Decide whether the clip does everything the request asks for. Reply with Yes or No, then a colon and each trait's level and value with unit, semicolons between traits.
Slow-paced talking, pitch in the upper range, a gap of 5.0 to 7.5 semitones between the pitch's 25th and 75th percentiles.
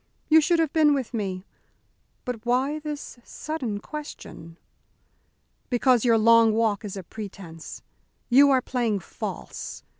Yes: slow, 130 wpm; high, 240 Hz; wide, 5.4 semitones